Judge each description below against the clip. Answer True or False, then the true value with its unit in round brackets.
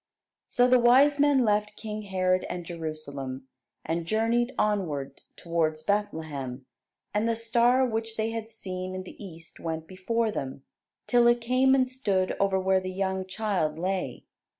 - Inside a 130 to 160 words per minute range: True (155 wpm)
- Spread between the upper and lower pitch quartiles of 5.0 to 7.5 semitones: True (5.4 semitones)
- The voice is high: True (195 Hz)